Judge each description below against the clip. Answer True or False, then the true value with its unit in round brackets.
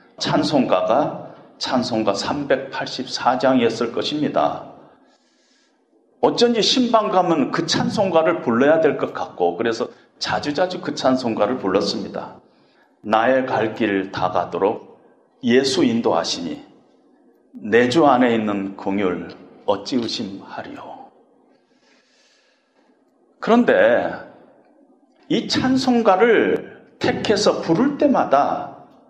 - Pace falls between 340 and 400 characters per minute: False (200 characters per minute)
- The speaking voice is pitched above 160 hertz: True (190 Hz)